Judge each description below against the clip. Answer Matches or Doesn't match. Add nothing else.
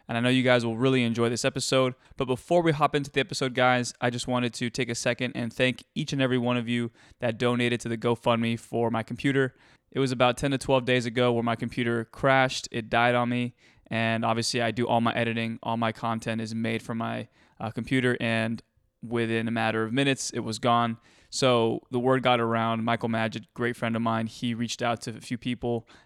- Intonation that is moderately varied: Doesn't match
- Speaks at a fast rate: Matches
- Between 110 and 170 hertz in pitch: Matches